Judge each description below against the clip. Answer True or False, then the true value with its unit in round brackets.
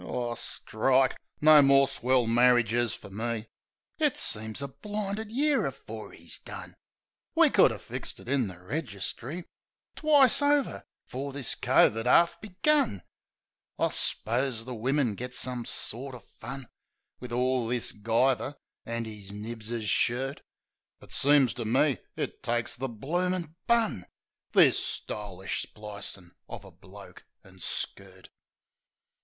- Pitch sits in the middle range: False (125 Hz)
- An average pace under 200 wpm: True (135 wpm)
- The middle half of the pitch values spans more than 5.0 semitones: False (4.1 semitones)